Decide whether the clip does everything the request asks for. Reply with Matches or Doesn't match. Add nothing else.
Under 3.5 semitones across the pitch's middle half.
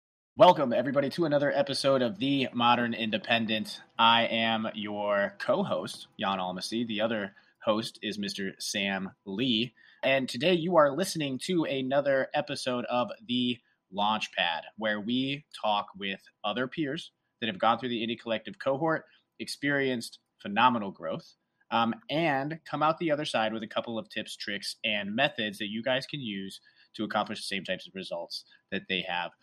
Doesn't match